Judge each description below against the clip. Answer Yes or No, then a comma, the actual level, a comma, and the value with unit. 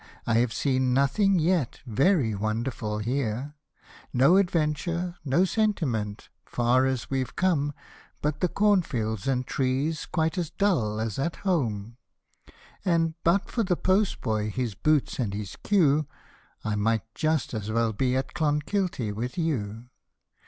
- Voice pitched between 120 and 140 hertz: Yes, low, 135 Hz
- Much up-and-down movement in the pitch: Yes, wide, 6.8 semitones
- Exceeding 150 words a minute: No, average, 140 wpm